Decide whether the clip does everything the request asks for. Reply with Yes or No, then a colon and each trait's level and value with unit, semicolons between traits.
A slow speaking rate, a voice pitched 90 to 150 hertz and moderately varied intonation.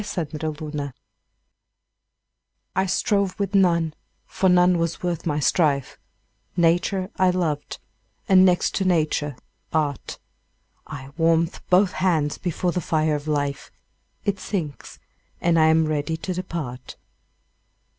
No: slow, 125 wpm; medium, 165 Hz; average, 3.3 semitones